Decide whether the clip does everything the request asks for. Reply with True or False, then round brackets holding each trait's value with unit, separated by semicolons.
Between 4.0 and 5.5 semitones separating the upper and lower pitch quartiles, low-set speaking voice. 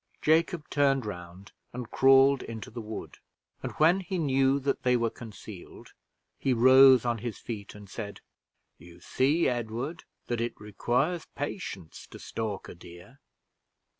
True (4.5 semitones; 120 Hz)